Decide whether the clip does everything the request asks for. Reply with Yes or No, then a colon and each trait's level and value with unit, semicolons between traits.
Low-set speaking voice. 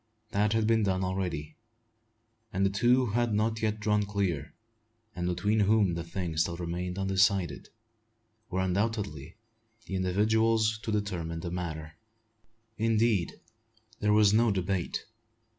Yes: low, 100 Hz